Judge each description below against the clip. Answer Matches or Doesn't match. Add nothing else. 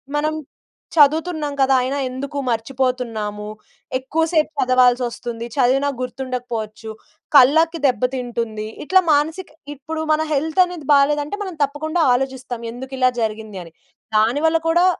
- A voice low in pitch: Doesn't match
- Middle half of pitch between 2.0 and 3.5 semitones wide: Doesn't match